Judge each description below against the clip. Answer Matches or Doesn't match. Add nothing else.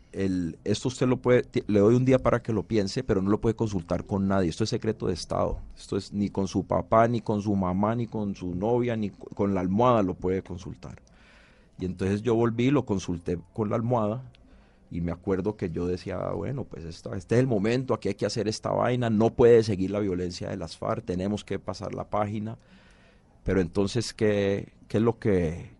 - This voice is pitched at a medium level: Doesn't match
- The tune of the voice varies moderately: Matches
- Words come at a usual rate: Doesn't match